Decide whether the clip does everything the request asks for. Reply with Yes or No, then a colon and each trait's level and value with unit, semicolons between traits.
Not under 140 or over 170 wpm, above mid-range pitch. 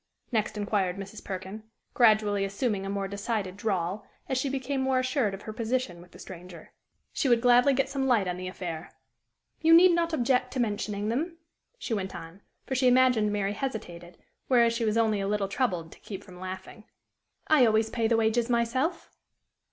No: average, 190 wpm; high, 220 Hz